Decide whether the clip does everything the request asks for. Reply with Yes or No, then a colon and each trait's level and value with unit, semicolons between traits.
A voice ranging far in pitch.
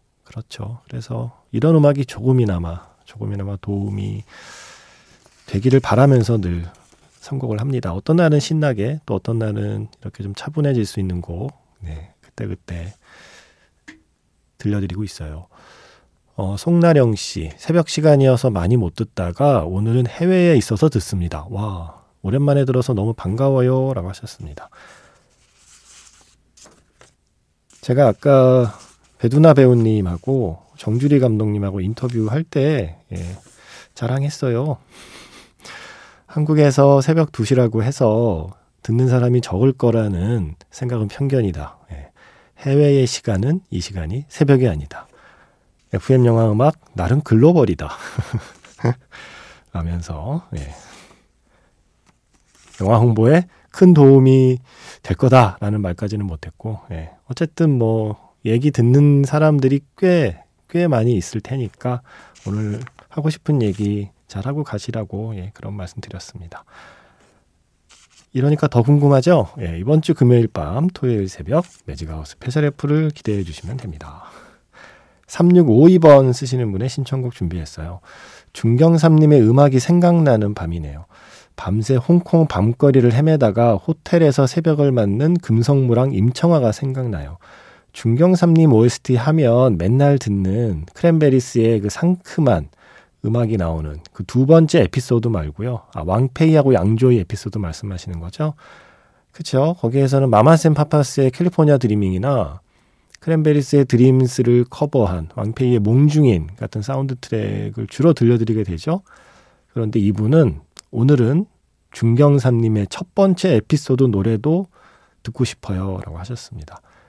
Yes: wide, 6.0 semitones